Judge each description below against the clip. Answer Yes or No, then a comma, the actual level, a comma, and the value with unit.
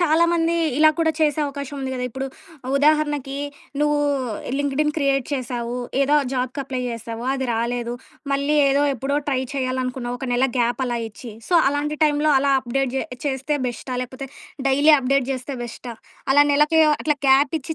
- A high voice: Yes, very high, 270 Hz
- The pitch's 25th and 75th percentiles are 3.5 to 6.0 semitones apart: No, average, 2.7 semitones